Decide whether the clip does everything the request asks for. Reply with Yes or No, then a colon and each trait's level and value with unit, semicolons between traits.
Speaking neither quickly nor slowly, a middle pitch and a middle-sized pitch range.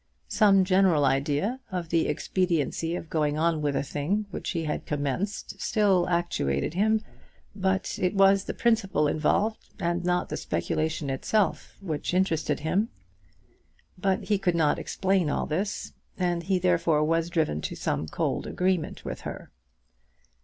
Yes: average, 150 wpm; medium, 175 Hz; average, 3.8 semitones